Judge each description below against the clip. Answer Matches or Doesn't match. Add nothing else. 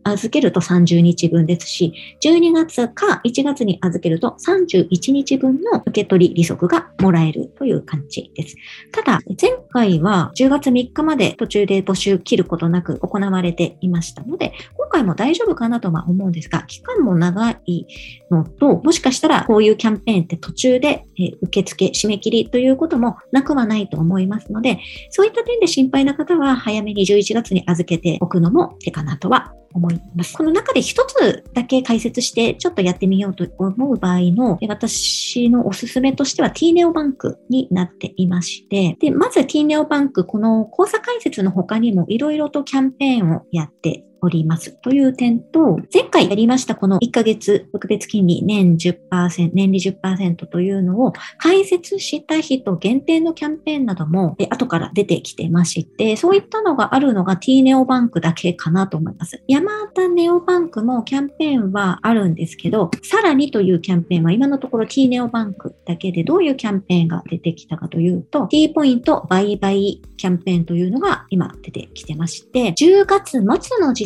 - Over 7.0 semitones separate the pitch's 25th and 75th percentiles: Matches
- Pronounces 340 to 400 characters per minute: Matches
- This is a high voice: Matches